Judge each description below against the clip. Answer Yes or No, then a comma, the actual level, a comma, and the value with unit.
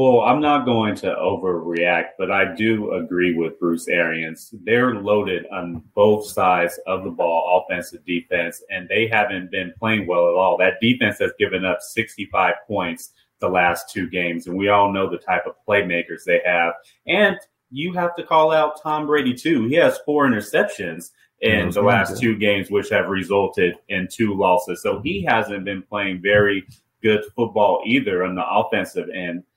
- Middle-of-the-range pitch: No, low, 100 Hz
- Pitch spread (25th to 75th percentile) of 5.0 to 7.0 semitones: Yes, wide, 5.5 semitones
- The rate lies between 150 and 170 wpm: No, average, 180 wpm